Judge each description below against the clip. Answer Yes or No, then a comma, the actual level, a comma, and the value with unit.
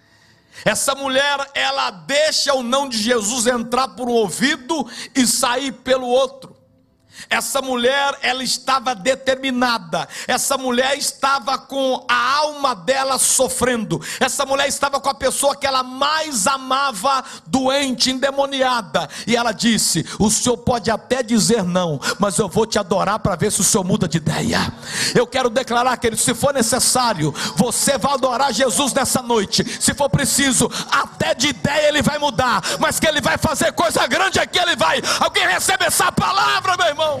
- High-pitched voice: Yes, very high, 255 Hz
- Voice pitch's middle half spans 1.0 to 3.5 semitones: Yes, average, 2.9 semitones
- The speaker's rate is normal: Yes, average, 165 wpm